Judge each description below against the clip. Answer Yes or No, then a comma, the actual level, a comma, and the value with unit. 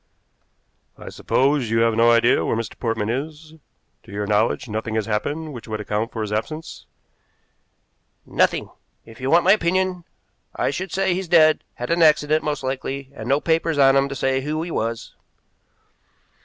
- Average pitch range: No, wide, 5.7 semitones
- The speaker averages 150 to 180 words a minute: Yes, average, 175 wpm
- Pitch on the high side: No, low, 135 Hz